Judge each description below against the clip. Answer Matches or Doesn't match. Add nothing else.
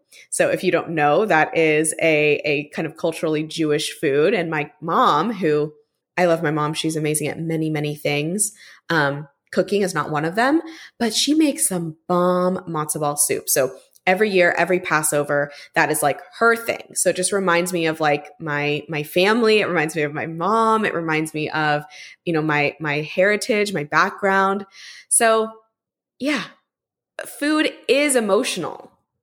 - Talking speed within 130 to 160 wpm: Doesn't match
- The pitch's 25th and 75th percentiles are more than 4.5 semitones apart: Matches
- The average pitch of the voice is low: Doesn't match